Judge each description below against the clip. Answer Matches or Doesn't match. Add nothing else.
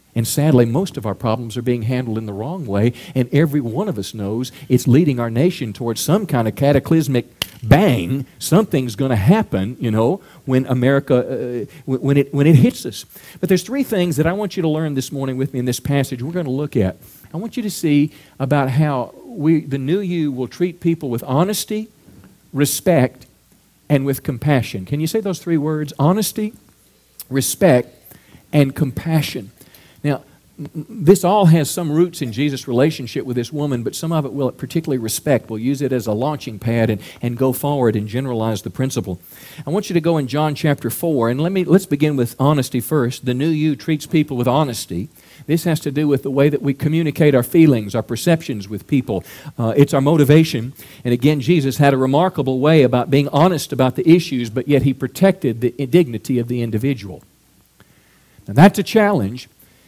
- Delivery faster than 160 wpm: Matches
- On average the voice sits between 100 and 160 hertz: Matches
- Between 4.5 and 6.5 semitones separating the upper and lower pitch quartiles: Doesn't match